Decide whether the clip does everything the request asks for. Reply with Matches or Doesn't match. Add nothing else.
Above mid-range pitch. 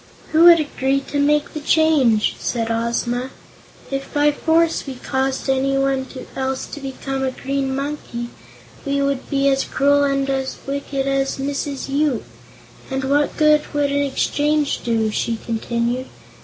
Matches